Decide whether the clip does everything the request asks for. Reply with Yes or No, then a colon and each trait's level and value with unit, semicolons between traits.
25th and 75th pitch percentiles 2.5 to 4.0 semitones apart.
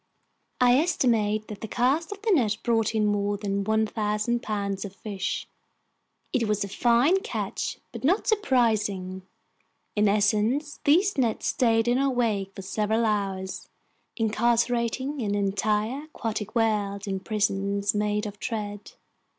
Yes: average, 2.9 semitones